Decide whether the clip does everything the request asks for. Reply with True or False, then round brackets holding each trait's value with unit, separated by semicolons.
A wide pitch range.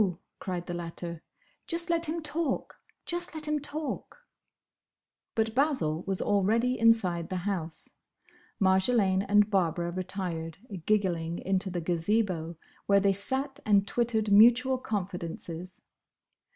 True (5.9 semitones)